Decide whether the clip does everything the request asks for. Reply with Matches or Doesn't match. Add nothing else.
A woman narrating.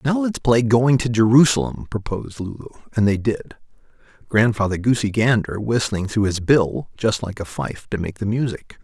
Doesn't match